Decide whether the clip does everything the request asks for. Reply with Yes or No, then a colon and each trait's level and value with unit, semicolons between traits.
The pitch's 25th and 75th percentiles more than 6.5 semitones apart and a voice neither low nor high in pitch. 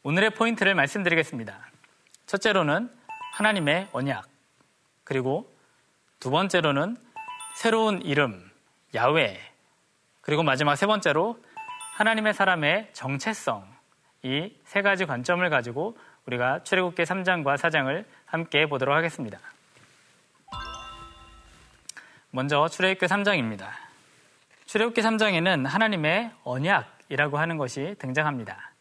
Yes: wide, 7.3 semitones; medium, 165 Hz